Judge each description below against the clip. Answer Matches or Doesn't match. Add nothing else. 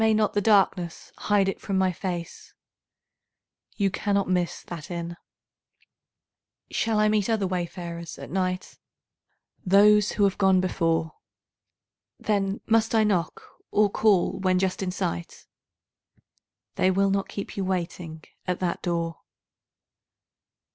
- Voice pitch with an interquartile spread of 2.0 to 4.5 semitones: Matches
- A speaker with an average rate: Doesn't match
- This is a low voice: Doesn't match